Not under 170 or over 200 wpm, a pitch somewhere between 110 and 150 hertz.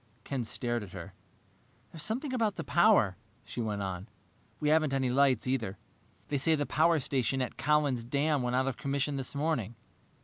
Yes: average, 180 wpm; low, 135 Hz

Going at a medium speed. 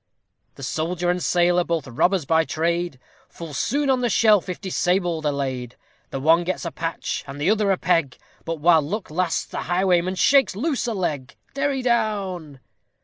Yes: average, 185 wpm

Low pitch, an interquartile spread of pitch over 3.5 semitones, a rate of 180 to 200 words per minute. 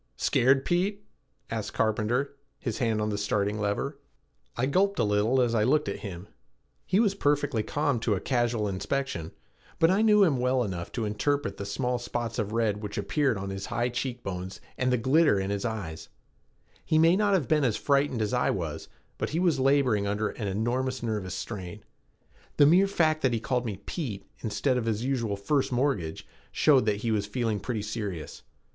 Yes: low, 120 Hz; average, 5.1 semitones; average, 190 wpm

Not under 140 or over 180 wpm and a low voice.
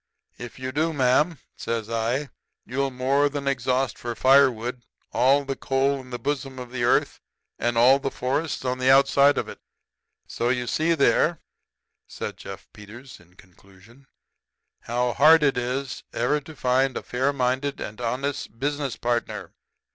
Yes: average, 160 wpm; low, 130 Hz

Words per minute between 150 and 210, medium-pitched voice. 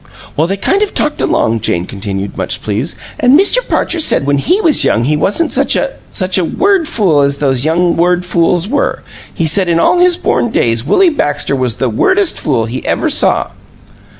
Yes: fast, 205 wpm; medium, 170 Hz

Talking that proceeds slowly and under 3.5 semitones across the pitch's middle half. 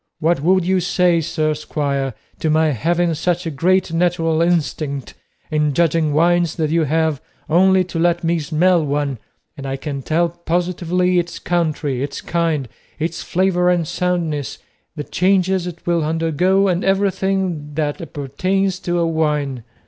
No: average, 155 wpm; average, 2.8 semitones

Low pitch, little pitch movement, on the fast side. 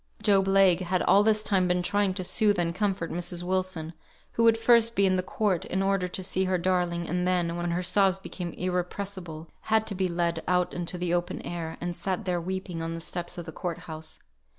No: medium, 180 Hz; narrow, 2.0 semitones; fast, 220 wpm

